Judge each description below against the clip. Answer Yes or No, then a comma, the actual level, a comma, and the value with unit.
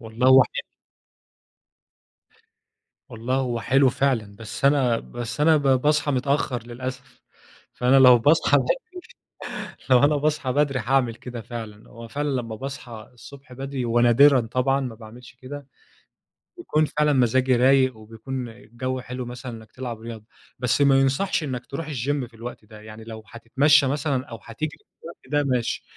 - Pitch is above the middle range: No, low, 130 Hz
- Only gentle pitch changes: No, average, 3.0 semitones